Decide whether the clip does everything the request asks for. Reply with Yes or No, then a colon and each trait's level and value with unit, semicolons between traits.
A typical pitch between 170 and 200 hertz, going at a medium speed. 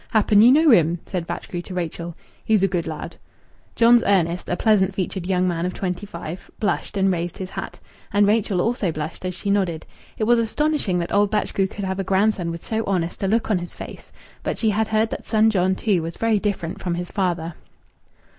No: high, 190 Hz; fast, 215 wpm